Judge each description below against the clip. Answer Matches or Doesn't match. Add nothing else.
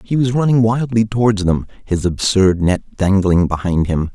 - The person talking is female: Doesn't match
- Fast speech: Doesn't match